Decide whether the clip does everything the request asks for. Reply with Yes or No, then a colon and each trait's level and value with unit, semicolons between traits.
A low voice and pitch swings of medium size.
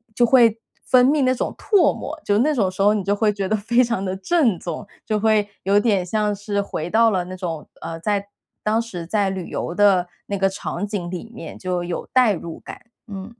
No: high, 205 Hz; average, 3.3 semitones